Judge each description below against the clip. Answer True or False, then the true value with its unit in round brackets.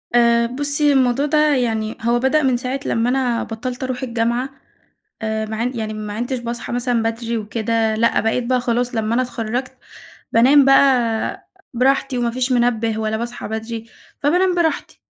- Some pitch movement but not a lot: False (2.3 semitones)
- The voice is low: False (240 Hz)